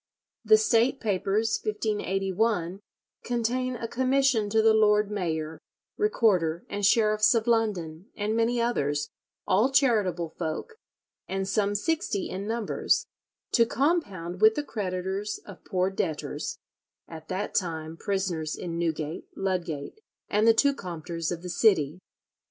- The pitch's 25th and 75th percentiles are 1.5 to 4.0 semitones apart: No, average, 4.6 semitones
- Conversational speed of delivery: No, slow, 130 wpm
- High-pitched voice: Yes, high, 205 Hz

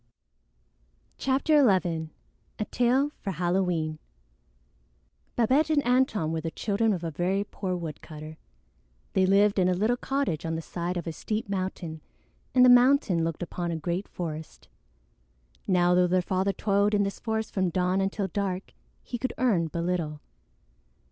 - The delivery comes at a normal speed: Yes, average, 155 wpm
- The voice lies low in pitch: No, medium, 185 Hz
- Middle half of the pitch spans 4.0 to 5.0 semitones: Yes, average, 4.4 semitones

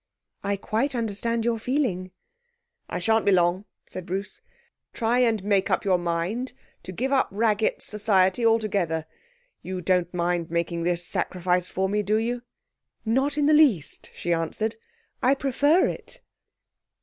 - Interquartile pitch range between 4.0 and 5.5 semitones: Yes, average, 4.5 semitones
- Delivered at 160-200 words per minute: No, average, 150 wpm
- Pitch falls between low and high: No, high, 205 Hz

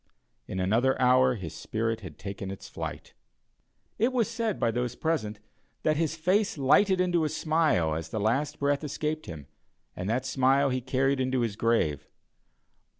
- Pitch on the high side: No, low, 130 Hz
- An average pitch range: No, wide, 6.3 semitones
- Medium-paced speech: Yes, average, 165 wpm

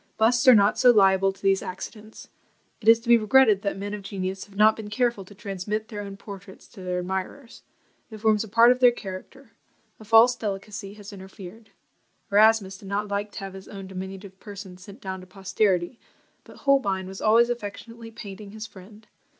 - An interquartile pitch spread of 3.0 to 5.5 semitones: No, narrow, 2.5 semitones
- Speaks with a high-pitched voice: Yes, high, 205 Hz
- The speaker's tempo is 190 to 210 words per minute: Yes, average, 195 wpm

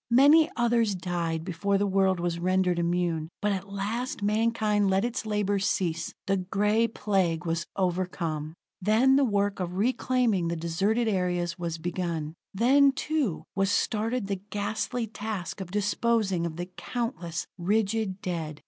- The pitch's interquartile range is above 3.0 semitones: Yes, average, 4.0 semitones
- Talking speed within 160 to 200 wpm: No, average, 150 wpm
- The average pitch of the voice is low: No, high, 195 Hz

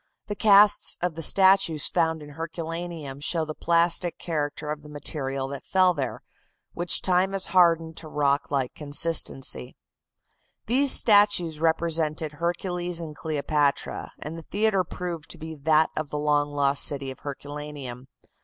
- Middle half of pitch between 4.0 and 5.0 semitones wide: No, average, 3.1 semitones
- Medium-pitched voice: Yes, medium, 160 Hz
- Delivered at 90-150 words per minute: Yes, average, 145 wpm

